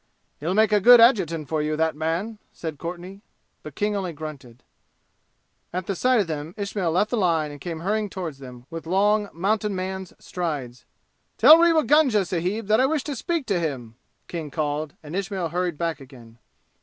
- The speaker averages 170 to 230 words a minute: Yes, average, 180 wpm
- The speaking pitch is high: No, medium, 180 Hz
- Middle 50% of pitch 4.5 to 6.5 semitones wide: Yes, average, 5.1 semitones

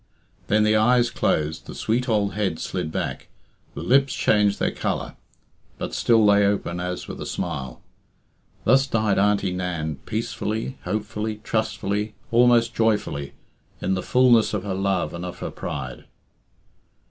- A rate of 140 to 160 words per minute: Yes, average, 145 wpm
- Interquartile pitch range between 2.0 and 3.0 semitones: No, average, 3.7 semitones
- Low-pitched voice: Yes, low, 105 Hz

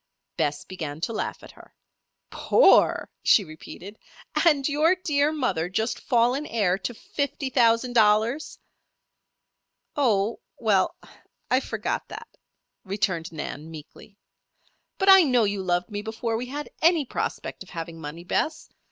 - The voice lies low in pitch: No, high, 220 Hz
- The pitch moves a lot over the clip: Yes, wide, 7.2 semitones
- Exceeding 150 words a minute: No, slow, 135 wpm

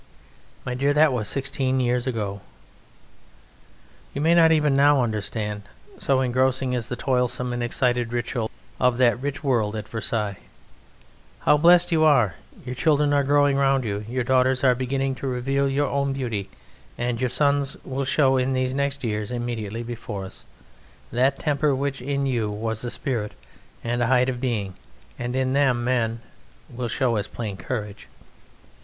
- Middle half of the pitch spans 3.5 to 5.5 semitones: No, average, 2.8 semitones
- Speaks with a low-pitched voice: Yes, low, 125 Hz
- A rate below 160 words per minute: No, average, 165 wpm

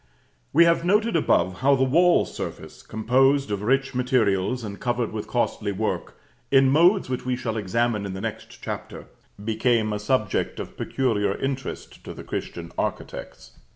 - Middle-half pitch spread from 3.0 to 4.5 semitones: Yes, average, 4.2 semitones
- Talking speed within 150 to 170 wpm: Yes, average, 160 wpm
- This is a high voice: No, low, 125 Hz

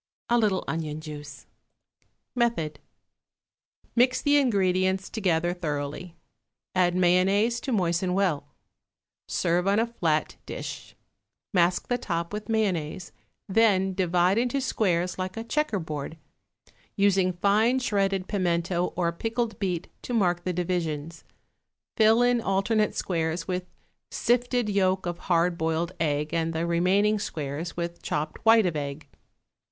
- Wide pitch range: No, average, 4.0 semitones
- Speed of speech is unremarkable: No, slow, 130 wpm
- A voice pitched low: No, medium, 185 Hz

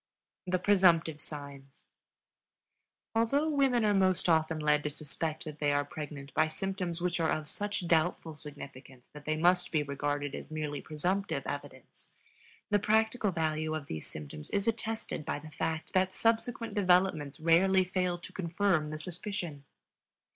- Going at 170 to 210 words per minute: No, average, 155 wpm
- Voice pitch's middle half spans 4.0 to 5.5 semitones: Yes, average, 4.3 semitones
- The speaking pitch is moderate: Yes, medium, 165 Hz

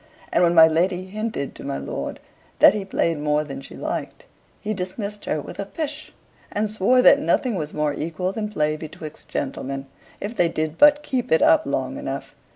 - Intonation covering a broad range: Yes, wide, 5.8 semitones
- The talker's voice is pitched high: No, medium, 180 Hz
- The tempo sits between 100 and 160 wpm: No, average, 195 wpm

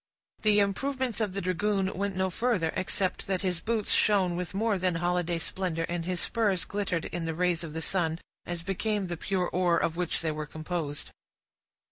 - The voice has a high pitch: No, medium, 180 Hz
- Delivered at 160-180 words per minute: No, average, 190 wpm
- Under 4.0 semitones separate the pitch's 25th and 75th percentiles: Yes, average, 2.9 semitones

